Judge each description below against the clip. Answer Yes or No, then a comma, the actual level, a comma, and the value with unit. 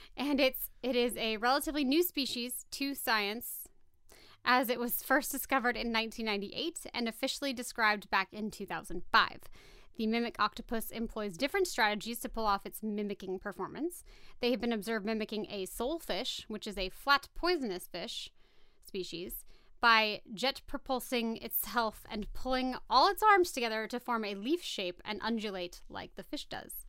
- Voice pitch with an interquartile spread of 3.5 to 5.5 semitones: Yes, average, 3.9 semitones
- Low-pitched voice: No, high, 230 Hz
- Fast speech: No, average, 160 wpm